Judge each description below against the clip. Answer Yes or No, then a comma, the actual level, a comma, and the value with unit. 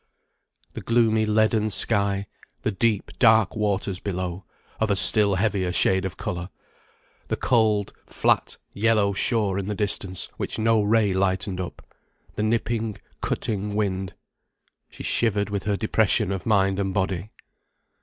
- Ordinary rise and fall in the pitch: No, narrow, 2.3 semitones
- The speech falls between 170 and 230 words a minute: No, average, 140 wpm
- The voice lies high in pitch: No, low, 100 Hz